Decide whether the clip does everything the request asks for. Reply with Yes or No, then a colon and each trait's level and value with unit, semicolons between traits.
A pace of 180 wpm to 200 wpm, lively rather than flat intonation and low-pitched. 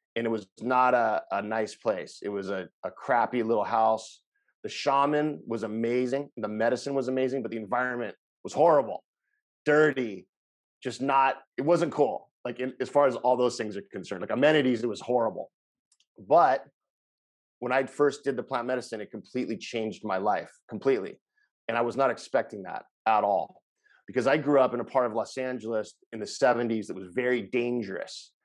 No: average, 185 wpm; average, 3.4 semitones; low, 125 Hz